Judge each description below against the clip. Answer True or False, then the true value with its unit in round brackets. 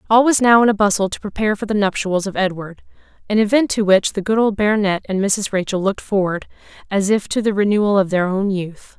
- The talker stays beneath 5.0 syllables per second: False (6.1 syllables/s)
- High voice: True (200 Hz)